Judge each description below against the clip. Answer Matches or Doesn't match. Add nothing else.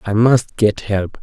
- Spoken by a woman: Doesn't match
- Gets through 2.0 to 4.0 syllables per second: Matches